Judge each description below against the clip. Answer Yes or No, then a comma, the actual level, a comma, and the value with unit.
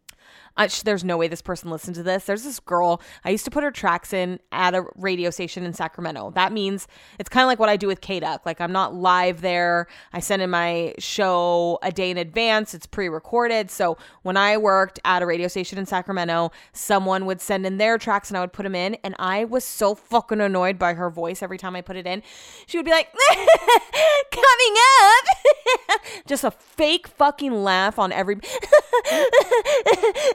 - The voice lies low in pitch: No, high, 195 Hz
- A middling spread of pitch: No, wide, 6.0 semitones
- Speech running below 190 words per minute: No, fast, 205 wpm